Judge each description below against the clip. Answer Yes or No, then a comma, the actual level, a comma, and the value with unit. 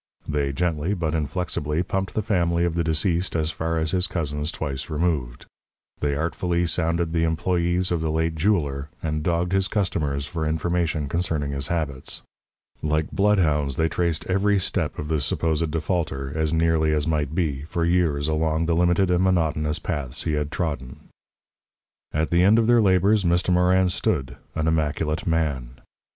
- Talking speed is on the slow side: No, average, 165 wpm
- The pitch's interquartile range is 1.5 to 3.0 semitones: Yes, narrow, 2.6 semitones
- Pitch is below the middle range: Yes, very low, 80 Hz